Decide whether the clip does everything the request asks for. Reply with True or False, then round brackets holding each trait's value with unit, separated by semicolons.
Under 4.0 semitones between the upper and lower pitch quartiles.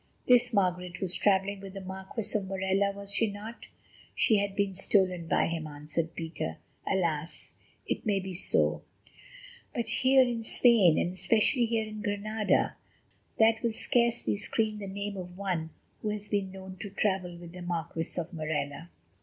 True (3.2 semitones)